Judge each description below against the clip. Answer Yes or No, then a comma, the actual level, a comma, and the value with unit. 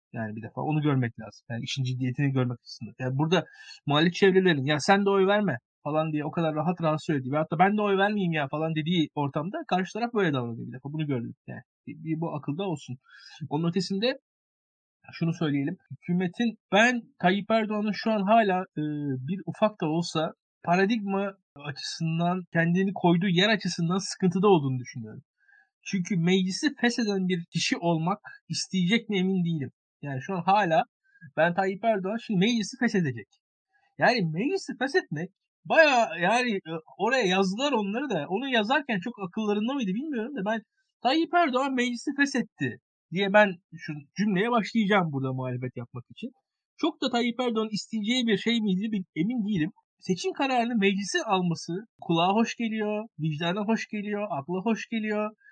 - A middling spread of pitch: No, wide, 5.9 semitones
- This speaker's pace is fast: Yes, fast, 160 wpm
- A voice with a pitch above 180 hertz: Yes, high, 190 Hz